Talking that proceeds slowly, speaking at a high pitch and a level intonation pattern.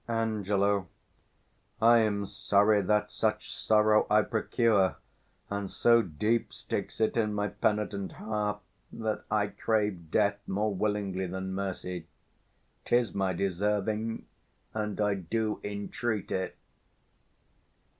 No: slow, 115 wpm; low, 105 Hz; narrow, 1.7 semitones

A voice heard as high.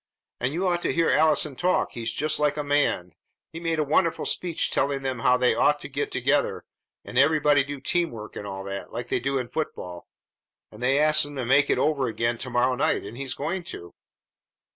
No: medium, 140 Hz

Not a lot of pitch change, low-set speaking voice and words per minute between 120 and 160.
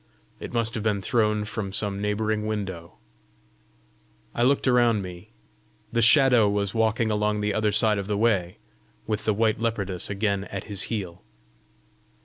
Yes: narrow, 2.1 semitones; low, 105 Hz; average, 155 wpm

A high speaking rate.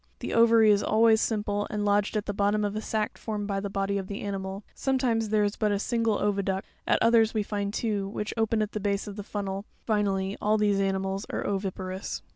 Yes: fast, 235 wpm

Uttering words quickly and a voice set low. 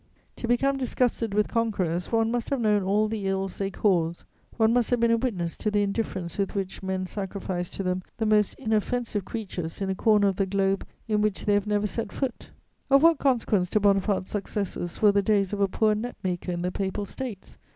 No: fast, 215 wpm; high, 205 Hz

